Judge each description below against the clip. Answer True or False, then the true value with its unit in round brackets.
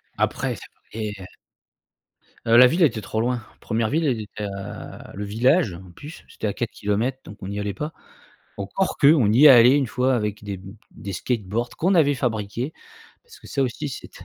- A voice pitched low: True (115 Hz)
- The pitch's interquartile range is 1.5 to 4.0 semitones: False (5.0 semitones)